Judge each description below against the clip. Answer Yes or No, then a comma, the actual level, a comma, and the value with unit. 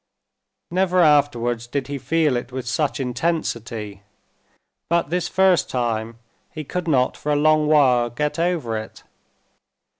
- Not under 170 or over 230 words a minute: No, average, 140 wpm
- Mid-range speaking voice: Yes, medium, 145 Hz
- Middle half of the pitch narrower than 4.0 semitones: No, average, 5.1 semitones